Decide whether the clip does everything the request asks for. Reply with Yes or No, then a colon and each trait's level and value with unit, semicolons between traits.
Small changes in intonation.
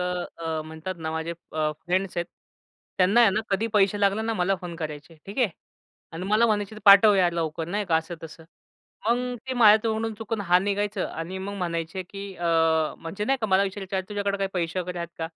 No: average, 3.4 semitones